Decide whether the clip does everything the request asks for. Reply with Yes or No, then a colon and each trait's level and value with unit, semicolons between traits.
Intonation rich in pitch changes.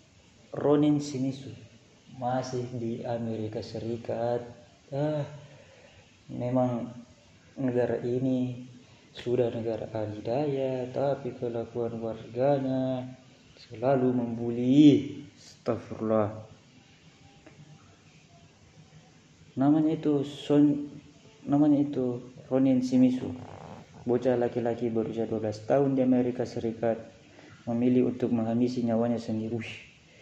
No: average, 2.7 semitones